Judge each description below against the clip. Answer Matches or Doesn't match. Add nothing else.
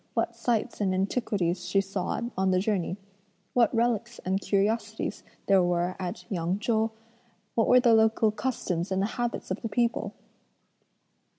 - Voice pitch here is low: Doesn't match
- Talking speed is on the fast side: Doesn't match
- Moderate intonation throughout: Matches